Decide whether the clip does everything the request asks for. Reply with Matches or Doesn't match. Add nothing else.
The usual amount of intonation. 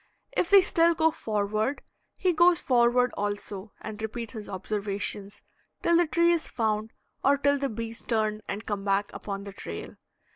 Doesn't match